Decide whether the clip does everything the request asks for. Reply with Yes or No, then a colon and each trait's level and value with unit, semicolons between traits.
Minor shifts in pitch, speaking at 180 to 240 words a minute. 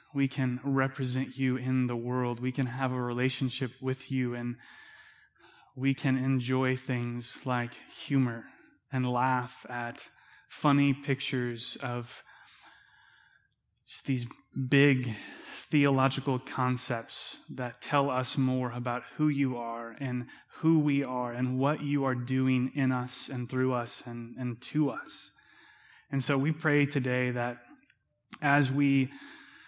No: narrow, 2.2 semitones; slow, 135 wpm